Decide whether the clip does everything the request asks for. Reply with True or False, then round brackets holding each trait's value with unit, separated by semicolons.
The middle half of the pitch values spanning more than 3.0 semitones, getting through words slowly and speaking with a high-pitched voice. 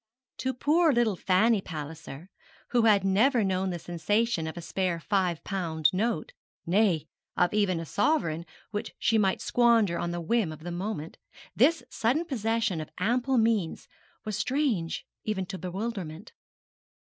False (5.0 semitones; 150 wpm; 195 Hz)